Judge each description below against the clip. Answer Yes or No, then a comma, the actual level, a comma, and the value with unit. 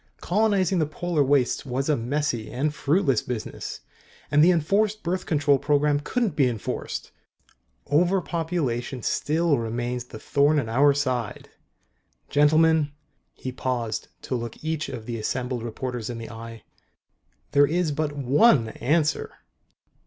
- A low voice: No, medium, 145 Hz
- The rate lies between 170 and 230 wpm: No, average, 140 wpm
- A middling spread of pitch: Yes, average, 4.5 semitones